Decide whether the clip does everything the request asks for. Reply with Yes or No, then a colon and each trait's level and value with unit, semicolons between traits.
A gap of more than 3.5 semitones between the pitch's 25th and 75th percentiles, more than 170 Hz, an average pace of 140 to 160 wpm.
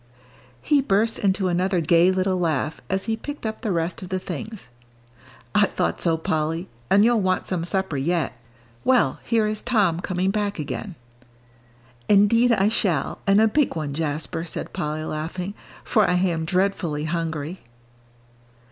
Yes: average, 4.1 semitones; medium, 185 Hz; average, 155 wpm